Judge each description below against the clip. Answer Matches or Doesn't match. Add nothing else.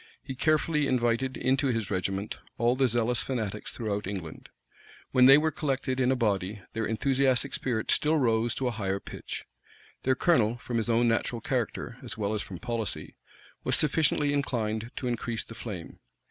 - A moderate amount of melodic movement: Matches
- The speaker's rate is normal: Matches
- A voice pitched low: Matches